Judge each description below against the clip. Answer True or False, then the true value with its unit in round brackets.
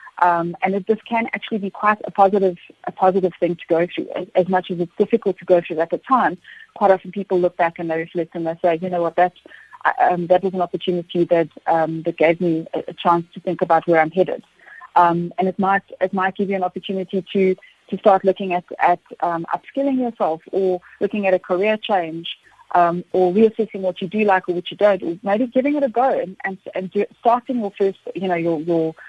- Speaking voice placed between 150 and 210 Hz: True (185 Hz)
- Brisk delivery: True (235 wpm)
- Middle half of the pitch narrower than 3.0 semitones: True (2.6 semitones)